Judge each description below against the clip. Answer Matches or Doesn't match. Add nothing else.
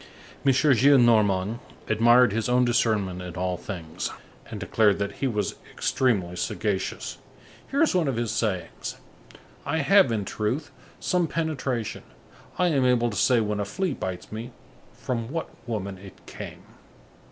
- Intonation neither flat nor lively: Matches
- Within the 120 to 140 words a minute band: Doesn't match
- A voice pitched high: Doesn't match